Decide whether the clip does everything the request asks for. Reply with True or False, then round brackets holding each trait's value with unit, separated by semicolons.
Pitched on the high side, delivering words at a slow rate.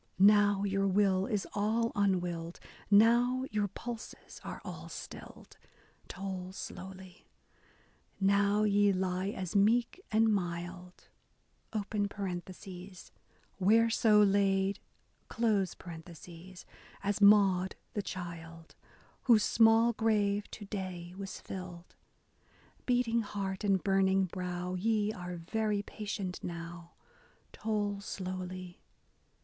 True (195 Hz; 100 wpm)